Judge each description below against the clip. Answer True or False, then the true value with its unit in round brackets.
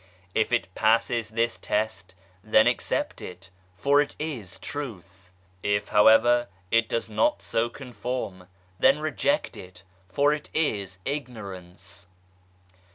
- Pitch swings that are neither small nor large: True (4.6 semitones)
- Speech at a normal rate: False (120 wpm)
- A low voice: True (110 Hz)